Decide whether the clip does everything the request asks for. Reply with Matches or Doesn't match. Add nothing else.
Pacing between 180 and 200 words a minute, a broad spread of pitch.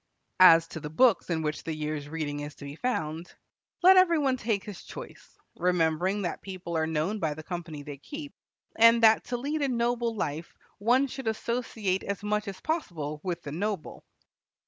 Matches